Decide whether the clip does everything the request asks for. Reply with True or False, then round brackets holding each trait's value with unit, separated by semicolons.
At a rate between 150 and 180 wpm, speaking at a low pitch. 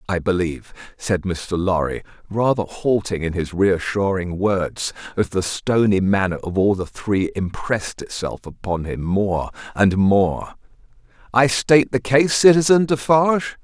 False (140 wpm; 105 Hz)